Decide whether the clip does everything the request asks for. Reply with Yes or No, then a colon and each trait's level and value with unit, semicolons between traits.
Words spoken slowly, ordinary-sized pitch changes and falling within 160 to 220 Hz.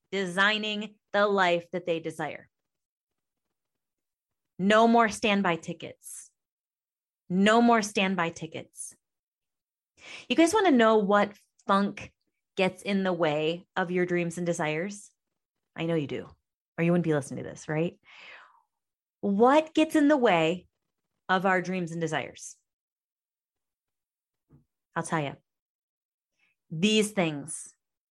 Yes: slow, 120 wpm; average, 4.3 semitones; medium, 185 Hz